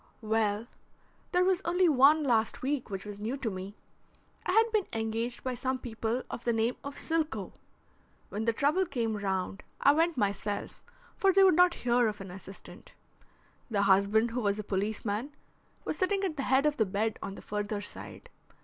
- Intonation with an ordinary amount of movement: No, wide, 6.2 semitones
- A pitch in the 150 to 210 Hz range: No, high, 230 Hz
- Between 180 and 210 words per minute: Yes, average, 185 wpm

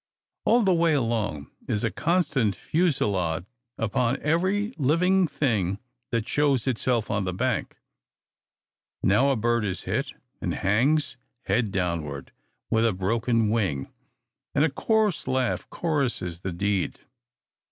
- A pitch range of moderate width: No, wide, 7.1 semitones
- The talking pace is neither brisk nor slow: No, slow, 130 wpm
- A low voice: Yes, low, 115 Hz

